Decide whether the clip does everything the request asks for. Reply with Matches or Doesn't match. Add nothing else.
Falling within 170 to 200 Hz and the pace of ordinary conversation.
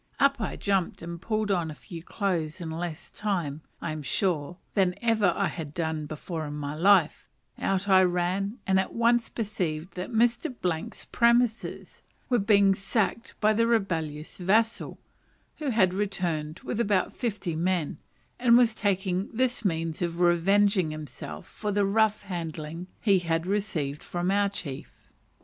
Matches